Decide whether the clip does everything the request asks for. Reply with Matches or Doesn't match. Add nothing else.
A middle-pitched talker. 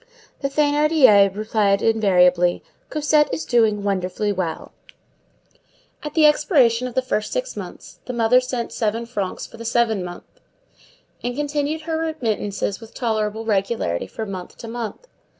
Doesn't match